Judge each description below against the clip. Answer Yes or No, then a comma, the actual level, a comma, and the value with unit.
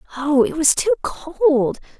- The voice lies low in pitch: No, very high, 315 Hz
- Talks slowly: No, average, 150 wpm